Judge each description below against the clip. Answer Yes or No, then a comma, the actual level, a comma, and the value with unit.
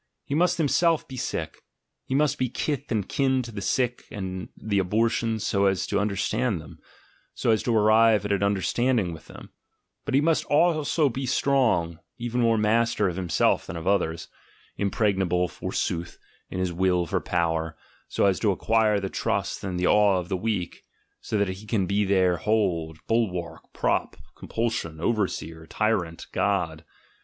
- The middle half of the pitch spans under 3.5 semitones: No, average, 4.5 semitones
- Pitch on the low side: Yes, low, 100 Hz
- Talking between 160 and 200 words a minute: Yes, average, 170 wpm